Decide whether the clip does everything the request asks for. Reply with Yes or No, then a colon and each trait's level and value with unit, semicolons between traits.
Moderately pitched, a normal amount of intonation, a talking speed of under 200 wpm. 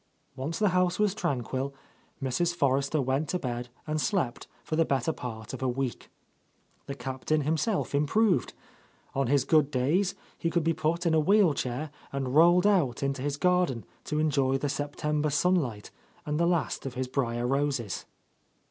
Yes: medium, 145 Hz; average, 4.2 semitones; average, 170 wpm